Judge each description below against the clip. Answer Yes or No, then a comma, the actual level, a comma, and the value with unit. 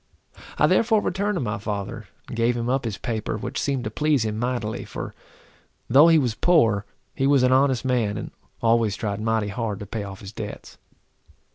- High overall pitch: No, low, 115 Hz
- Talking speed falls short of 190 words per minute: No, average, 195 wpm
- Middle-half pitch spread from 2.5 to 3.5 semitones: No, average, 4.0 semitones